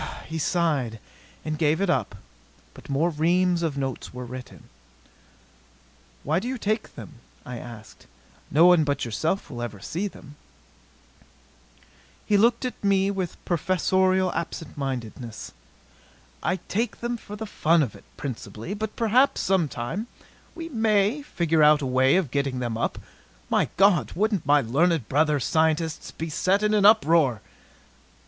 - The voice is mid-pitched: Yes, medium, 165 Hz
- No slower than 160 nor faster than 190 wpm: No, average, 150 wpm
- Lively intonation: Yes, wide, 6.2 semitones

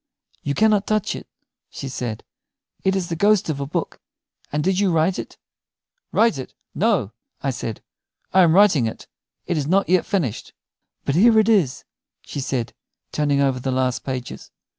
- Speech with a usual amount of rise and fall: No, wide, 6.8 semitones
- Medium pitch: Yes, medium, 155 Hz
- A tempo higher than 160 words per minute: Yes, average, 175 wpm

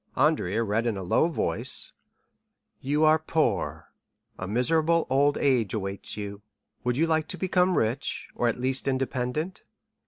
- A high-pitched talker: No, low, 130 Hz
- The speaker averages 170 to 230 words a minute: No, average, 150 wpm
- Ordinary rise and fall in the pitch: No, wide, 5.8 semitones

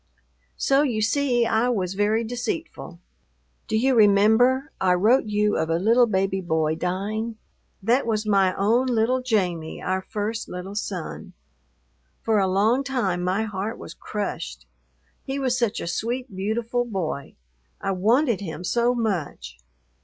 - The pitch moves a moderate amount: Yes, average, 4.2 semitones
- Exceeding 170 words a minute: No, average, 145 wpm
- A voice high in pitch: Yes, high, 215 Hz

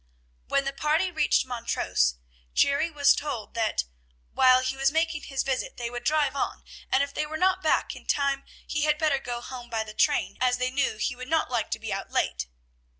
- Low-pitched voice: No, very high, 275 Hz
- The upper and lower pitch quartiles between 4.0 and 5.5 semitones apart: No, average, 3.5 semitones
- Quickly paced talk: Yes, fast, 210 wpm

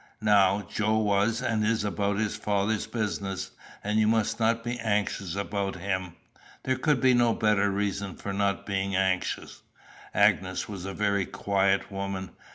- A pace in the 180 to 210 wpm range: No, average, 160 wpm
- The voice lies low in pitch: Yes, low, 100 Hz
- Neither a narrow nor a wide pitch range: No, narrow, 2.0 semitones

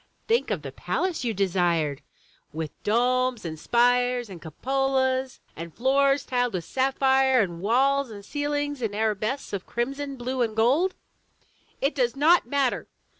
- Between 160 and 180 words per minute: No, average, 145 wpm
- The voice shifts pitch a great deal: No, average, 4.4 semitones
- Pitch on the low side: No, very high, 250 Hz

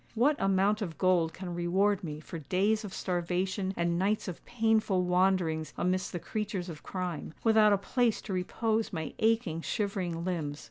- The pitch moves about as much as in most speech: Yes, average, 3.4 semitones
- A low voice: No, medium, 185 Hz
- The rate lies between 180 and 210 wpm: No, average, 170 wpm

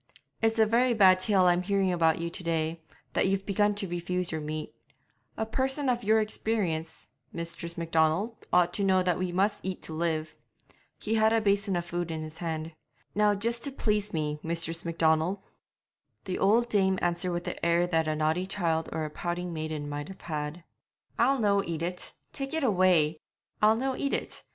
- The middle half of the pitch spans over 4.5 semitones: No, average, 4.1 semitones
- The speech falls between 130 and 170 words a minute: No, average, 195 wpm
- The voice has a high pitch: No, medium, 180 Hz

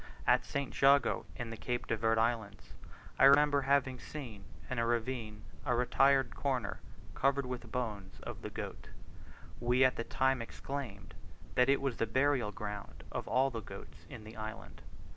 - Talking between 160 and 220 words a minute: Yes, average, 170 wpm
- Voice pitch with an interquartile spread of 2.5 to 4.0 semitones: Yes, average, 3.4 semitones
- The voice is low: Yes, low, 125 Hz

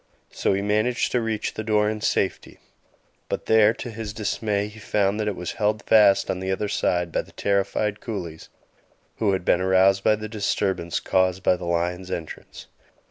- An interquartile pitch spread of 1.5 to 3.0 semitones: Yes, narrow, 2.5 semitones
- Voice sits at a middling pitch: No, low, 100 Hz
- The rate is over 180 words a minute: Yes, average, 190 wpm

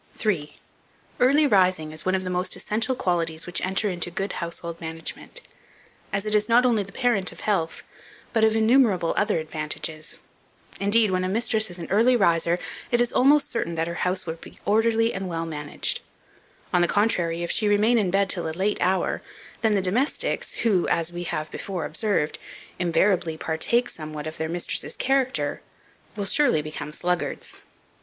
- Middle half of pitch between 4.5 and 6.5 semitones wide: Yes, average, 4.8 semitones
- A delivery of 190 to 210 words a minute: No, average, 180 wpm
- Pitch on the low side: No, medium, 185 Hz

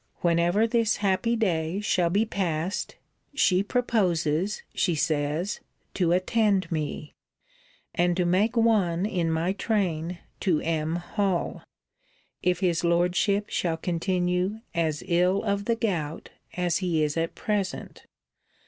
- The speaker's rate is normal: No, slow, 125 wpm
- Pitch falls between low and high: Yes, medium, 180 Hz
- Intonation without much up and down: No, average, 3.3 semitones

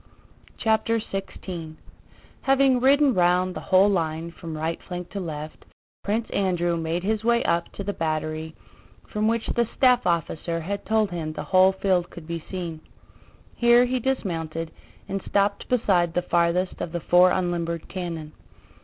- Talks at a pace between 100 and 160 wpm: Yes, average, 155 wpm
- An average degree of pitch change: Yes, average, 4.0 semitones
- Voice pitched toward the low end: No, medium, 180 Hz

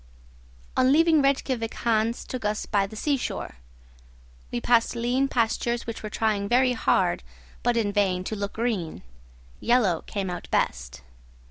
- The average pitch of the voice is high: Yes, high, 225 Hz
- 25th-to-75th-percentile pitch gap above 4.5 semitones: No, average, 3.5 semitones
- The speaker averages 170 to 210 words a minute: No, average, 145 wpm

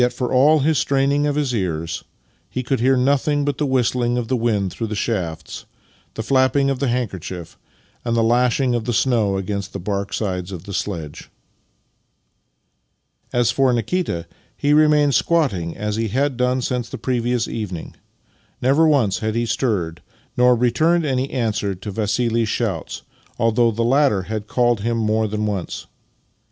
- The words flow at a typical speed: Yes, average, 165 wpm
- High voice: No, low, 120 Hz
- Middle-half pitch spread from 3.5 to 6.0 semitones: Yes, average, 4.3 semitones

